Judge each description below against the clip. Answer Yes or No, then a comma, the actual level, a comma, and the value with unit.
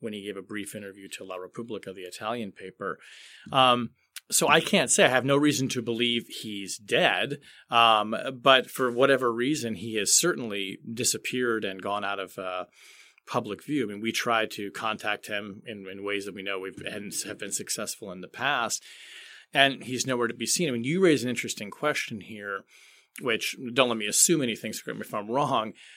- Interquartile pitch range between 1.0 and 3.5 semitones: No, average, 4.1 semitones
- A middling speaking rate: Yes, average, 195 wpm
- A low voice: Yes, low, 115 Hz